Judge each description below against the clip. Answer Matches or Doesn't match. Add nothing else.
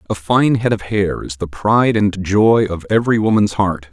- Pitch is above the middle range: Doesn't match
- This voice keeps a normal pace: Doesn't match